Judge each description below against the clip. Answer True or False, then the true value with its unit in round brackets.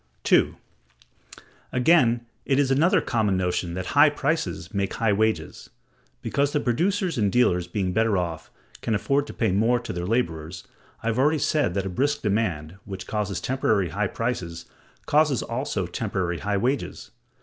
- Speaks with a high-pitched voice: False (110 Hz)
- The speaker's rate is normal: True (160 wpm)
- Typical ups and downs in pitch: False (6.3 semitones)